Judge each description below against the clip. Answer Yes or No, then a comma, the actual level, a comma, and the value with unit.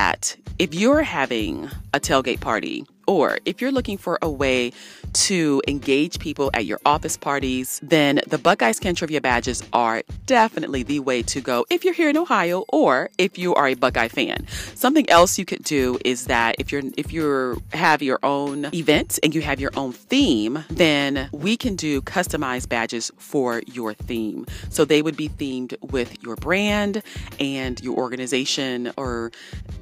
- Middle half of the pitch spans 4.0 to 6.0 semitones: Yes, wide, 5.5 semitones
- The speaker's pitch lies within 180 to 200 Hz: No, medium, 140 Hz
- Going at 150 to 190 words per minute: Yes, average, 175 wpm